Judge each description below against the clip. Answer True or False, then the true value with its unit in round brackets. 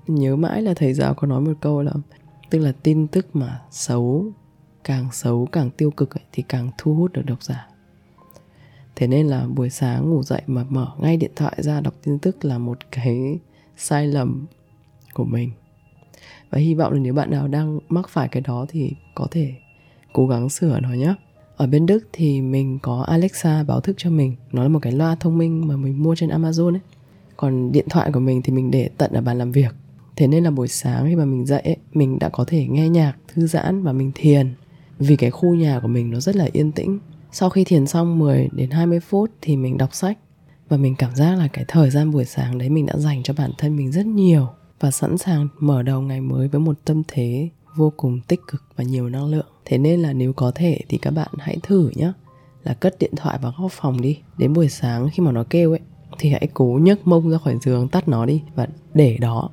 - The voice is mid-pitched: True (145 Hz)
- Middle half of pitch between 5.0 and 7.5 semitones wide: False (3.5 semitones)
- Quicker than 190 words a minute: True (235 wpm)